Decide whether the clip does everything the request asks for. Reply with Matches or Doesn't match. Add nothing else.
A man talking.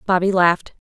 Doesn't match